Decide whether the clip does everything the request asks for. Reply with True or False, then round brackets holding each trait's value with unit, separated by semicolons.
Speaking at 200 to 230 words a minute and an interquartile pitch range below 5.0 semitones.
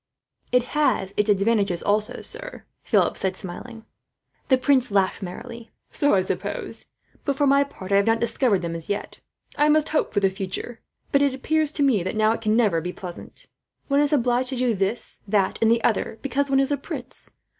False (205 wpm; 5.6 semitones)